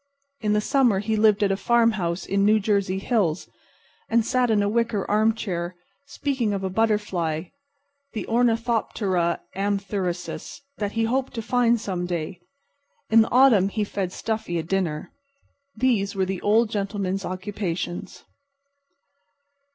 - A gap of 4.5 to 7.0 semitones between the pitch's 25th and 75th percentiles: No, average, 3.2 semitones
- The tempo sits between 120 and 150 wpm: Yes, average, 145 wpm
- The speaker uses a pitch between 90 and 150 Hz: No, high, 205 Hz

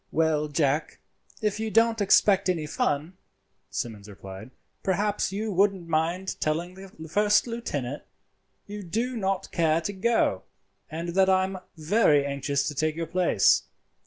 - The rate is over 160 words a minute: No, average, 145 wpm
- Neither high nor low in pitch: Yes, medium, 180 Hz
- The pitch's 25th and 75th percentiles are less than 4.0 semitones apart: No, average, 5.0 semitones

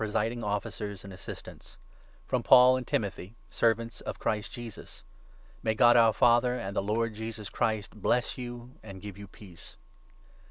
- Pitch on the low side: Yes, low, 110 Hz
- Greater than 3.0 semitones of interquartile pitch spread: No, narrow, 2.6 semitones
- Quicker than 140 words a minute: Yes, average, 160 wpm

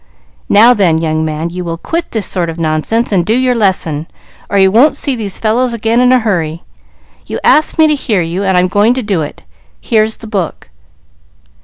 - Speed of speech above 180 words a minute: Yes, fast, 205 wpm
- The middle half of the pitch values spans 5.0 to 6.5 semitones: Yes, wide, 5.6 semitones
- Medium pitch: No, high, 200 Hz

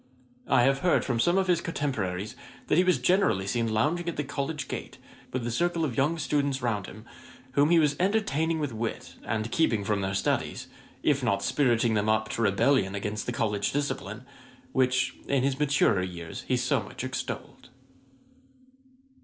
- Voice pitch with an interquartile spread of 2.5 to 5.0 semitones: No, wide, 5.4 semitones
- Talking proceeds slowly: No, average, 180 wpm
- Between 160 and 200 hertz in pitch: No, low, 130 Hz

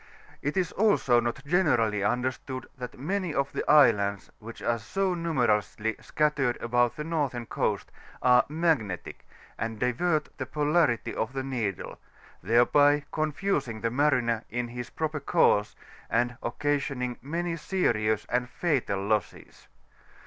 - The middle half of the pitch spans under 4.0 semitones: No, average, 4.6 semitones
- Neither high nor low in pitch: No, low, 125 Hz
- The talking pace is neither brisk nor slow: No, slow, 125 wpm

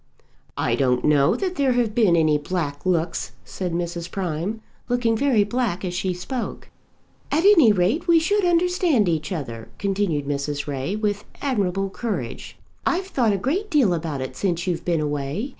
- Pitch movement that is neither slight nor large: No, wide, 7.2 semitones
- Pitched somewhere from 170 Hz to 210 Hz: Yes, high, 190 Hz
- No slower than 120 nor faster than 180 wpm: Yes, average, 170 wpm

